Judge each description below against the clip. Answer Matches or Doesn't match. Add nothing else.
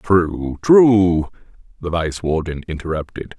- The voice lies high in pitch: Doesn't match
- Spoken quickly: Doesn't match